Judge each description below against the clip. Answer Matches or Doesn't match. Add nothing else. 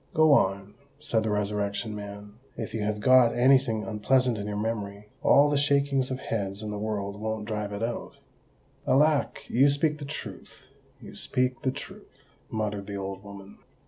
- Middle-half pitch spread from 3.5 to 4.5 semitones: Matches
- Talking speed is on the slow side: Doesn't match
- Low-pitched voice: Matches